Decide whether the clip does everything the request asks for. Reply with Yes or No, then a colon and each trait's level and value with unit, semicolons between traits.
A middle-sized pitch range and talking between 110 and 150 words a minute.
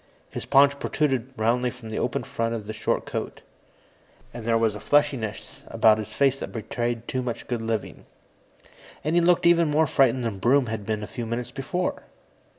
No: average, 3.6 semitones; average, 190 wpm